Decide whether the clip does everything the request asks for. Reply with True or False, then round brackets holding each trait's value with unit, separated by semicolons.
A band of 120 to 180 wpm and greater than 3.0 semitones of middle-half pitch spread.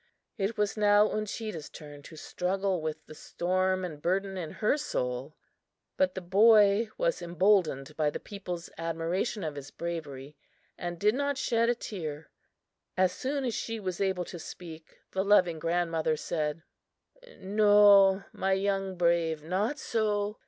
True (150 wpm; 4.1 semitones)